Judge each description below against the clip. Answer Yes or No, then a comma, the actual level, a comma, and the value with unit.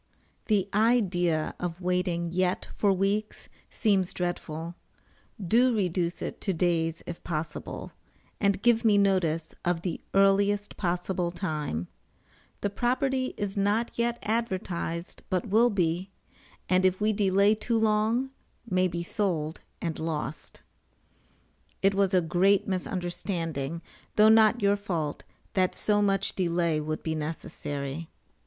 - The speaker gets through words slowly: Yes, slow, 130 wpm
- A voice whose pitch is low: No, medium, 185 Hz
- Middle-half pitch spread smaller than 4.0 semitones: Yes, average, 3.4 semitones